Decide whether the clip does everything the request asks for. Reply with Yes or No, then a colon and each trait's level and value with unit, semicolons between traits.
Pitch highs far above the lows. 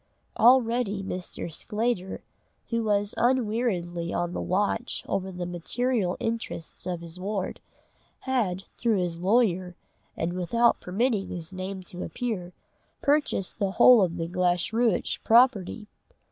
No: average, 4.5 semitones